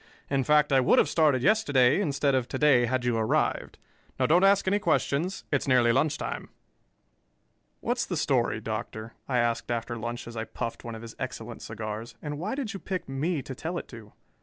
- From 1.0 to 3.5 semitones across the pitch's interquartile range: No, average, 4.7 semitones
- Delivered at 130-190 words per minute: No, fast, 205 wpm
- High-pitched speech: No, low, 130 Hz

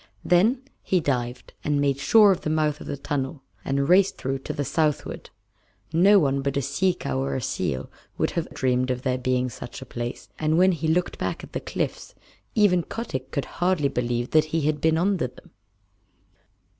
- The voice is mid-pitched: Yes, medium, 145 Hz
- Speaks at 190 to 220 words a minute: Yes, average, 195 wpm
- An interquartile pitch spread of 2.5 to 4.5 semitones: No, average, 4.9 semitones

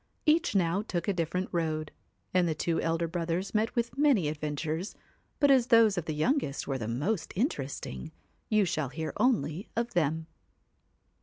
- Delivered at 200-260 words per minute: No, average, 165 wpm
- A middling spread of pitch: No, wide, 5.8 semitones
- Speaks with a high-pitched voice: No, medium, 170 Hz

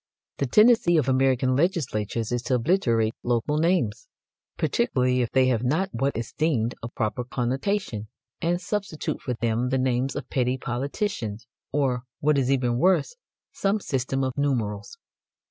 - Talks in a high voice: No, low, 130 Hz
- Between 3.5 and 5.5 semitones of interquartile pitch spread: Yes, average, 4.5 semitones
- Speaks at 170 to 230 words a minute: No, average, 150 wpm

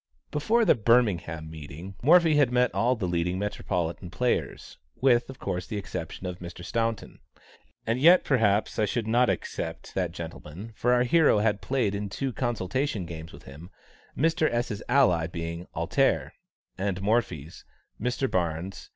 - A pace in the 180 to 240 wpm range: No, average, 155 wpm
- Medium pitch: No, low, 105 Hz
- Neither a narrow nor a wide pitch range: No, wide, 6.1 semitones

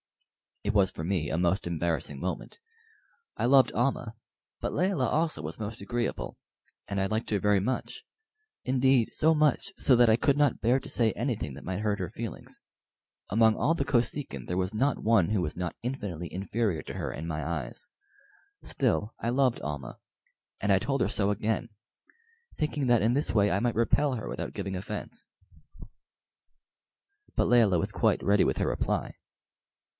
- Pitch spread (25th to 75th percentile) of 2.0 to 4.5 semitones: No, average, 5.3 semitones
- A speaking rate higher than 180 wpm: No, average, 175 wpm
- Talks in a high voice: No, low, 110 Hz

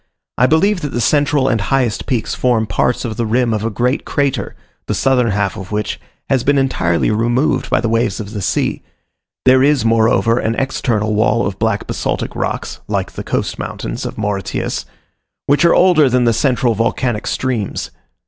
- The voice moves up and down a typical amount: Yes, average, 3.5 semitones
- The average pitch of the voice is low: Yes, low, 120 Hz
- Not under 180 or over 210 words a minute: Yes, average, 185 wpm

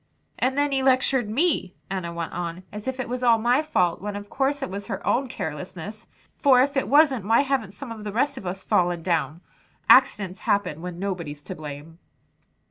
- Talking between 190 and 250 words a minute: Yes, fast, 205 wpm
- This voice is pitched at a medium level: No, high, 210 Hz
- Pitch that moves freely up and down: Yes, wide, 6.8 semitones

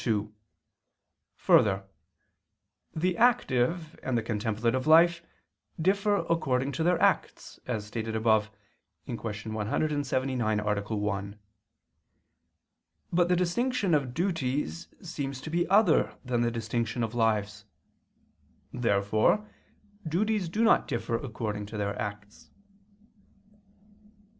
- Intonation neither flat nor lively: No, wide, 7.6 semitones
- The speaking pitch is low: Yes, low, 125 Hz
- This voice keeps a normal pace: No, slow, 105 wpm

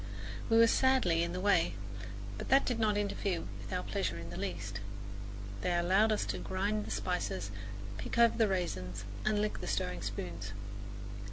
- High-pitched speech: No, medium, 180 Hz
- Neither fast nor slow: Yes, average, 175 wpm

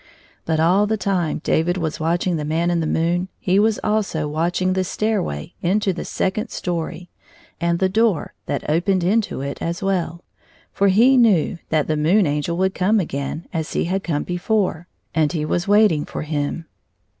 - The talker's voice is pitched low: No, medium, 175 Hz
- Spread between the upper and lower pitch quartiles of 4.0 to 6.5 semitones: No, average, 3.4 semitones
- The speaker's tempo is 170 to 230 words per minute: Yes, average, 180 wpm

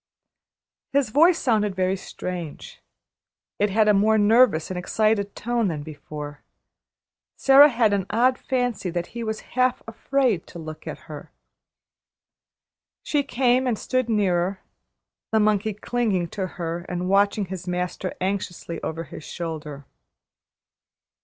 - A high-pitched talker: Yes, high, 200 Hz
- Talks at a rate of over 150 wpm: No, slow, 135 wpm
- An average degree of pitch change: Yes, average, 5.0 semitones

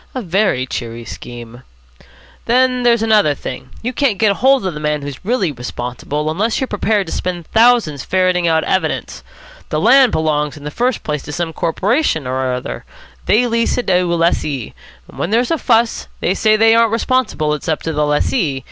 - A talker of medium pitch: Yes, medium, 180 Hz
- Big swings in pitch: Yes, wide, 7.5 semitones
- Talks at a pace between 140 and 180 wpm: No, average, 190 wpm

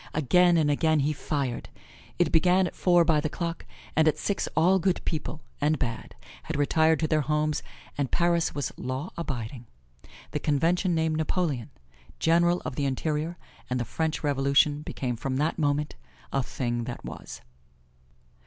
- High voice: No, medium, 155 Hz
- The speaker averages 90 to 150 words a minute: No, average, 160 wpm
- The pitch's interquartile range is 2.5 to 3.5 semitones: Yes, average, 3.2 semitones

